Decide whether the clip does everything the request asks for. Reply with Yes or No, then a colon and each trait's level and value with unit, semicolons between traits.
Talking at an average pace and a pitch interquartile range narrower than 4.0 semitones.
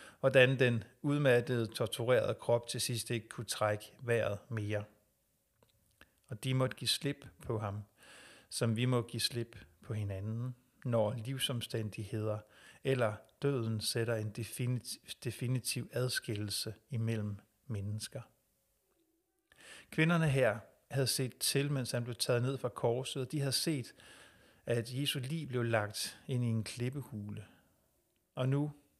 No: slow, 130 wpm; average, 3.3 semitones